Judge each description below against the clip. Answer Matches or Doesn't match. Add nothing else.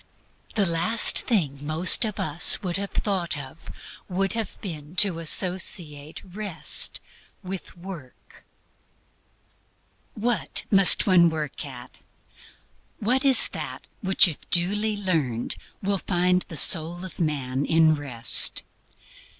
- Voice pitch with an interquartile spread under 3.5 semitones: Doesn't match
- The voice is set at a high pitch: Doesn't match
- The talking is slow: Matches